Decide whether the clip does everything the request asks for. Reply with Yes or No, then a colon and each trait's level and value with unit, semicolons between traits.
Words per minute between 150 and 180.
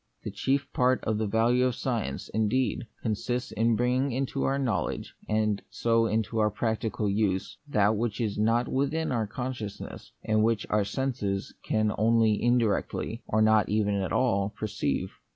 Yes: average, 160 wpm